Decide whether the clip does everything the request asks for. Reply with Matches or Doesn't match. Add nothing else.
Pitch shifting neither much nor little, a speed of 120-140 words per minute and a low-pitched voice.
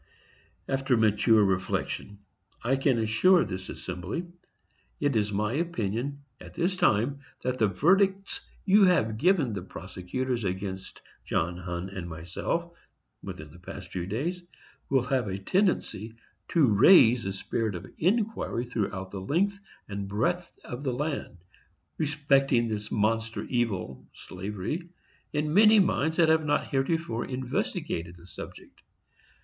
Doesn't match